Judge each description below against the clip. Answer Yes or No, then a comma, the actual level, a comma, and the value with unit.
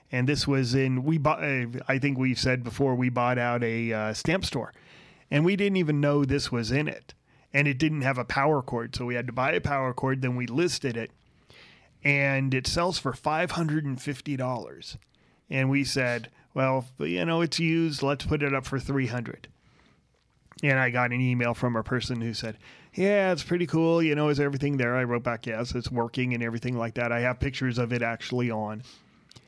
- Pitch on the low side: Yes, low, 130 Hz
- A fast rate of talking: Yes, fast, 220 wpm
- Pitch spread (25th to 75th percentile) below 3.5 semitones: Yes, average, 2.9 semitones